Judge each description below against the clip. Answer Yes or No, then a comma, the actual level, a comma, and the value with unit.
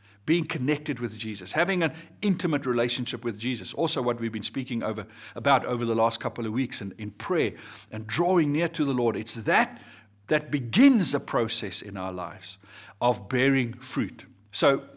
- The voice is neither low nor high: No, low, 120 Hz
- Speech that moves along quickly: No, average, 180 wpm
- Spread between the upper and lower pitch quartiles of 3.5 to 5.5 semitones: Yes, average, 5.1 semitones